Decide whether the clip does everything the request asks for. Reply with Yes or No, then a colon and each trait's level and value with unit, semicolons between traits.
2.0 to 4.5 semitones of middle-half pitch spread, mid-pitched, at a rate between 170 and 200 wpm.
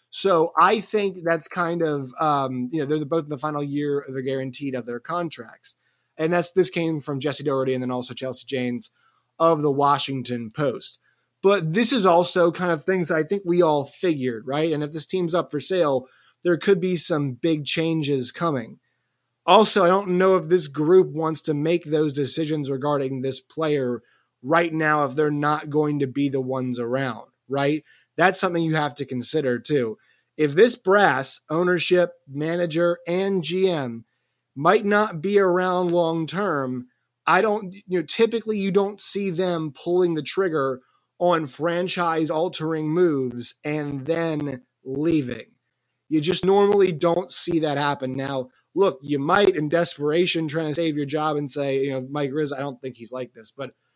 Yes: average, 4.2 semitones; medium, 155 Hz; average, 180 wpm